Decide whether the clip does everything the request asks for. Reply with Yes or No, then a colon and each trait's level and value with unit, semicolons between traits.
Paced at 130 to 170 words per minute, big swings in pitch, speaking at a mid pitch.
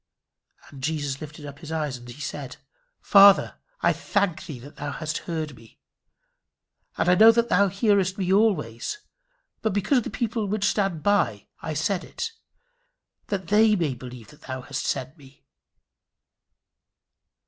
Yes: average, 155 wpm; wide, 6.3 semitones; medium, 160 Hz